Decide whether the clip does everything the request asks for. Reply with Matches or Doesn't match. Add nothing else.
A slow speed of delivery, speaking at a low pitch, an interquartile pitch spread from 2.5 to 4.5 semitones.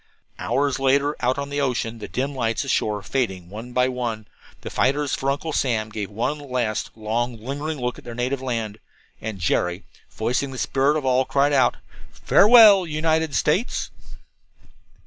Doesn't match